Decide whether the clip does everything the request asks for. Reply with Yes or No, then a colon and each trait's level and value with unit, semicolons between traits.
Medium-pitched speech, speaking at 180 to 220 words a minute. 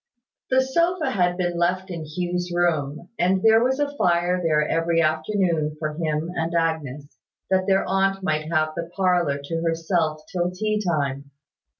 No: medium, 175 Hz; average, 165 wpm